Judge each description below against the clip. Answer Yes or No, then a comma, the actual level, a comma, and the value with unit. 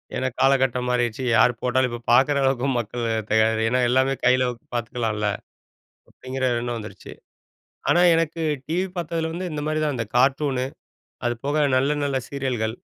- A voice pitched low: Yes, low, 130 Hz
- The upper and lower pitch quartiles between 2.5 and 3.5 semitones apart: Yes, average, 2.9 semitones